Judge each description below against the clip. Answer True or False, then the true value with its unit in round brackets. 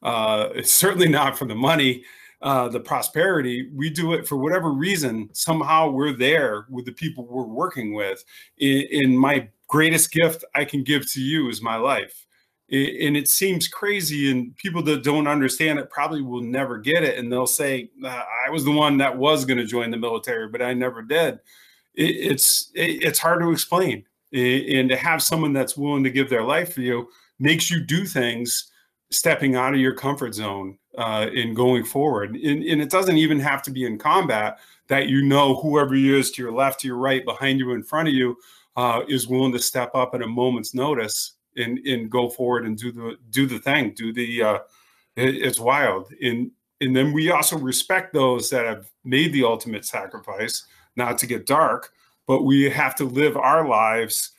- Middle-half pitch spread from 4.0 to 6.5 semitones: False (3.3 semitones)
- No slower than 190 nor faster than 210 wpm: True (195 wpm)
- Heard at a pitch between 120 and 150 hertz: True (135 Hz)